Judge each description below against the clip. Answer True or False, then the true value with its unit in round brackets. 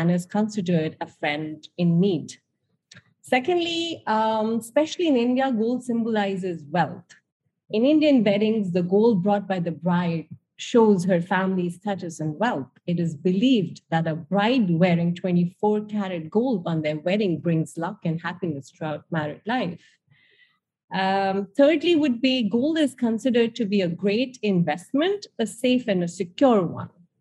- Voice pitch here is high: True (195 Hz)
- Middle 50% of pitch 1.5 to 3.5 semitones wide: False (5.5 semitones)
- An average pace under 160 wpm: True (150 wpm)